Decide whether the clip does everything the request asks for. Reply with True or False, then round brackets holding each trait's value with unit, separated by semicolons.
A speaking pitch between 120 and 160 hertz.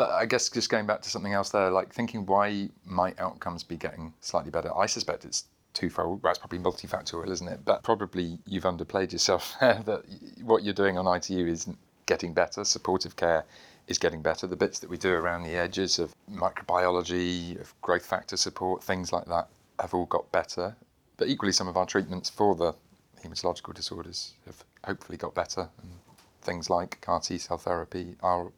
False (90 Hz)